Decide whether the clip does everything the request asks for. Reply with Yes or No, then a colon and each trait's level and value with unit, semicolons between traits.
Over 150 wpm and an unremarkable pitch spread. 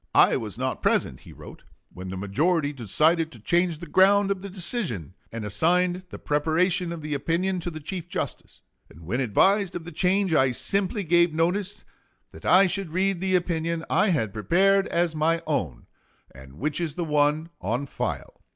Yes: average, 185 wpm; average, 4.3 semitones